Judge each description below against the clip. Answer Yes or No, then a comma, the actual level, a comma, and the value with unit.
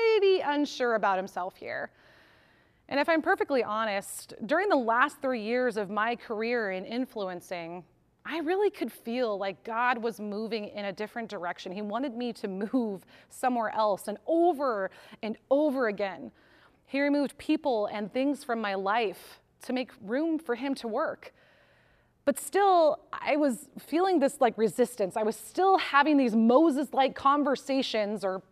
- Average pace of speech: Yes, average, 160 wpm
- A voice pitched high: Yes, high, 245 Hz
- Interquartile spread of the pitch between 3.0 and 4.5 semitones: No, average, 5.2 semitones